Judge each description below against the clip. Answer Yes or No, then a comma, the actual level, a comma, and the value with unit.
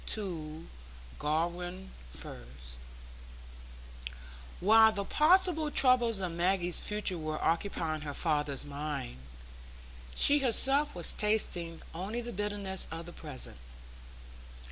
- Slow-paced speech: Yes, slow, 100 wpm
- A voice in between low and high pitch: Yes, medium, 180 Hz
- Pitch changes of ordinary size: No, wide, 5.7 semitones